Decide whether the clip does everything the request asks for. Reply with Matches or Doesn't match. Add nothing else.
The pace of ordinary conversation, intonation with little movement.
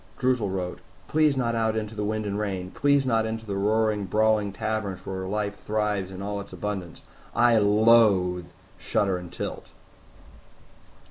Matches